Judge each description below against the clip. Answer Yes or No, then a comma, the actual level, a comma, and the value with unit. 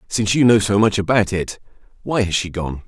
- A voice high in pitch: No, low, 100 Hz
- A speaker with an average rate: No, fast, 230 wpm